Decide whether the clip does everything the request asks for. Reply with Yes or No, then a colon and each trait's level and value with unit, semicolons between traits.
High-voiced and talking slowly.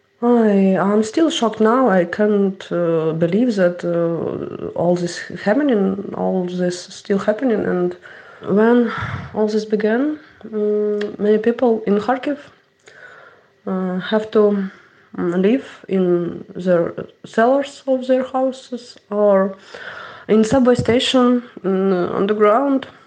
Yes: high, 210 Hz; slow, 110 wpm